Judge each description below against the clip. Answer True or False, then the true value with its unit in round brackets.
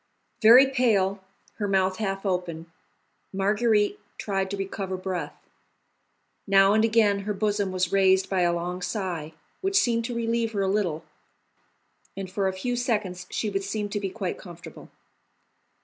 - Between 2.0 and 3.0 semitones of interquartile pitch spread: True (2.5 semitones)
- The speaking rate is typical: True (155 wpm)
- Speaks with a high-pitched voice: True (195 Hz)